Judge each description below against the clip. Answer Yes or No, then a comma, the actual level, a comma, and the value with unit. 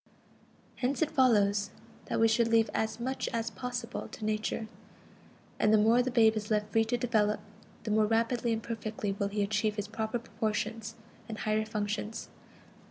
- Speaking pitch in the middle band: No, high, 220 Hz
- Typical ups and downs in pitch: No, narrow, 1.6 semitones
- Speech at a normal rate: Yes, average, 170 wpm